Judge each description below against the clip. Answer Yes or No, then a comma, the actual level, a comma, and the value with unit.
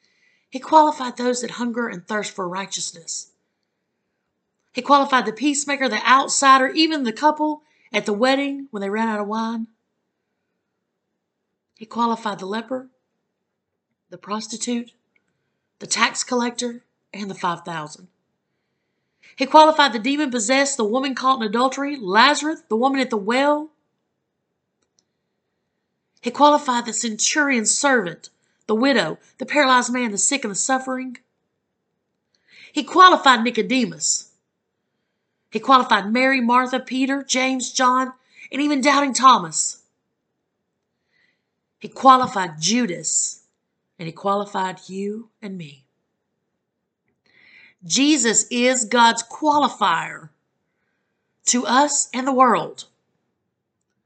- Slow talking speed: Yes, slow, 115 wpm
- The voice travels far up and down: No, average, 3.9 semitones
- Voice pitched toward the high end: Yes, high, 245 Hz